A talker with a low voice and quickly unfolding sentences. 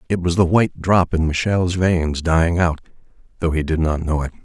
Yes: very low, 85 Hz; fast, 215 wpm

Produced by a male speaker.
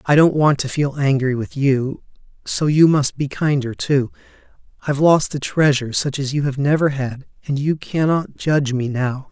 Yes: male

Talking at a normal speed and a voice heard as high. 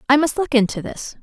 No: fast, 245 wpm; very high, 265 Hz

